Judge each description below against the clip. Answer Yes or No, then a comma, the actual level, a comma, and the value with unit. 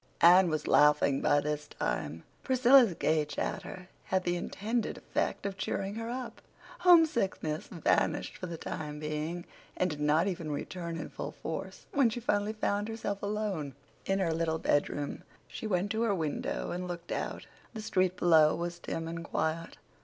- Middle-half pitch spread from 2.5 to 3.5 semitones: No, average, 4.8 semitones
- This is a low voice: No, medium, 175 Hz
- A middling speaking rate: Yes, average, 170 wpm